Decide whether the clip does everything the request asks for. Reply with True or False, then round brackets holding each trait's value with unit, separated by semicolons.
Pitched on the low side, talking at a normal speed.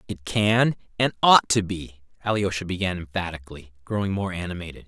True (95 Hz; 150 wpm)